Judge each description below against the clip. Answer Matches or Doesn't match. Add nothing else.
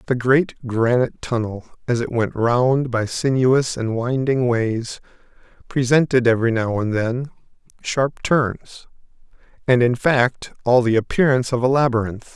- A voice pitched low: Matches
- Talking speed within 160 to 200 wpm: Doesn't match